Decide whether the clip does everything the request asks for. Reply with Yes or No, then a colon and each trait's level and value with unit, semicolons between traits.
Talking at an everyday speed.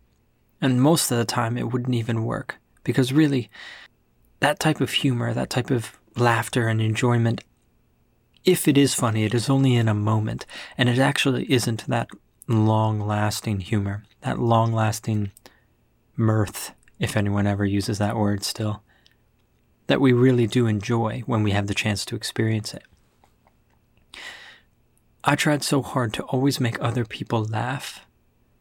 Yes: average, 155 wpm